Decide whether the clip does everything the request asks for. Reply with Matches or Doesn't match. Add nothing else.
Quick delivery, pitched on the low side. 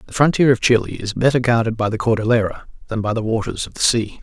Matches